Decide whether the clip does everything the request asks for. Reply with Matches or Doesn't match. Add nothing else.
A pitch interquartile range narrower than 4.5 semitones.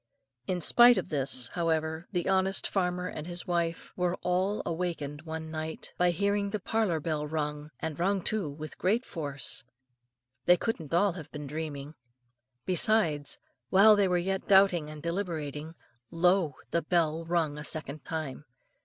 Matches